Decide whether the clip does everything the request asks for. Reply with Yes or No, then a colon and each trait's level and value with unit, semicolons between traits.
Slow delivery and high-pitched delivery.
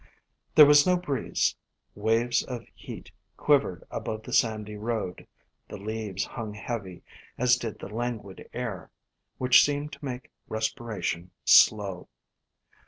No: slow, 130 wpm; low, 115 Hz